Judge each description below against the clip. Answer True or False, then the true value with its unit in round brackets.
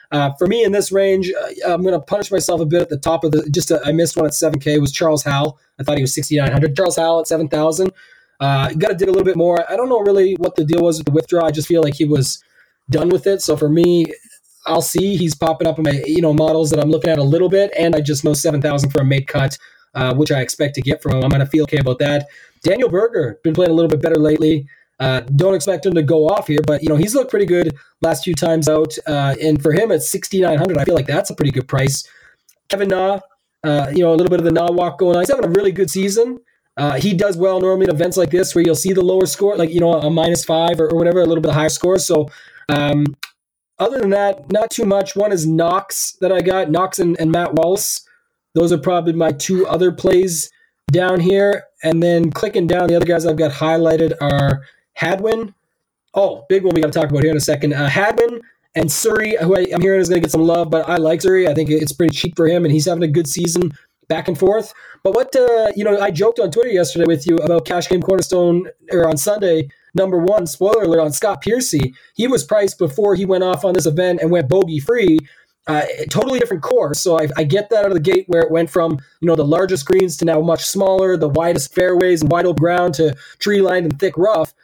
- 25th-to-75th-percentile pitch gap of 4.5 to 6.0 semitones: False (3.3 semitones)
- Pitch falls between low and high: True (170 Hz)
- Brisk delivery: True (260 wpm)